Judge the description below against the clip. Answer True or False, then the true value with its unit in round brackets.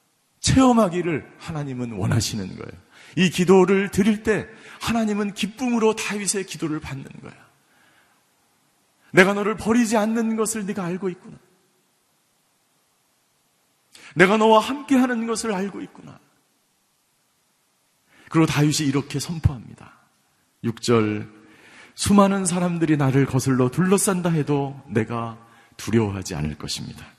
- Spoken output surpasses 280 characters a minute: False (265 characters per minute)